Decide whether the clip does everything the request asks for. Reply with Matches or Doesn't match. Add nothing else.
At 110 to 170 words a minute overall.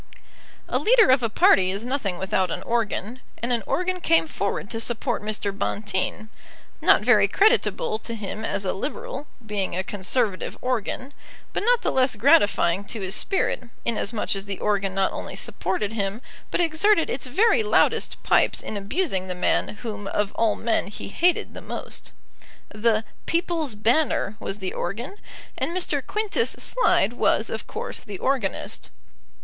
Matches